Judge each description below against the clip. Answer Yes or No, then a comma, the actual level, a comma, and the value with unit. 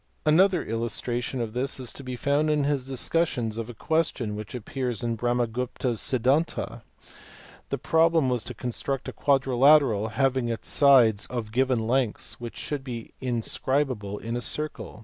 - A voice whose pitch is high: No, low, 125 Hz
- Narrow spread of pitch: No, average, 3.1 semitones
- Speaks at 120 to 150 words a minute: No, average, 160 wpm